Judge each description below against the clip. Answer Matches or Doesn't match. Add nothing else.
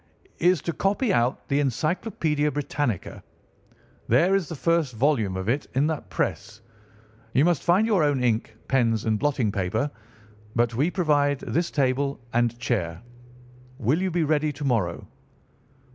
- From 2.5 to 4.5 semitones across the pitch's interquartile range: Doesn't match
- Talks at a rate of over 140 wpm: Matches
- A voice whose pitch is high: Doesn't match